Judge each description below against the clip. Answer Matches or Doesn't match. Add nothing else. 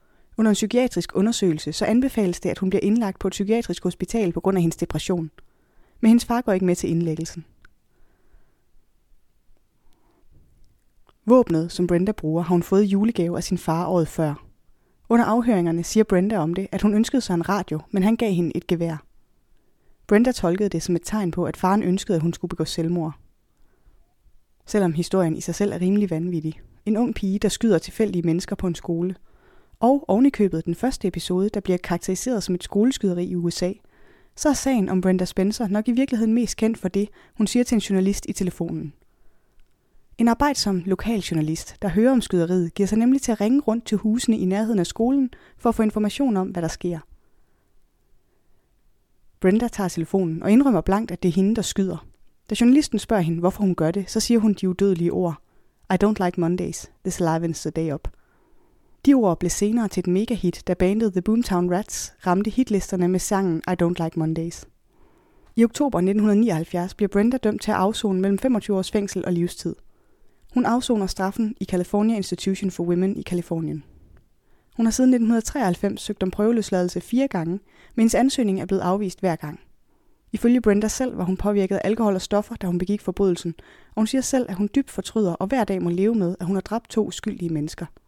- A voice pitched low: Doesn't match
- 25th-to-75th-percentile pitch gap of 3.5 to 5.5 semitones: Matches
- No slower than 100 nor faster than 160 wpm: Doesn't match